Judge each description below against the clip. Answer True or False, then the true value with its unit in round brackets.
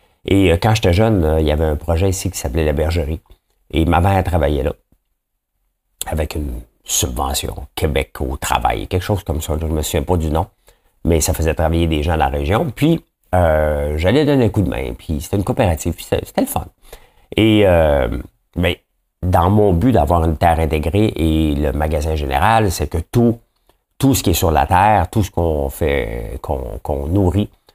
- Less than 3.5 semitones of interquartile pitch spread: False (4.1 semitones)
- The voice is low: True (85 Hz)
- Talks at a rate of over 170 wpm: True (200 wpm)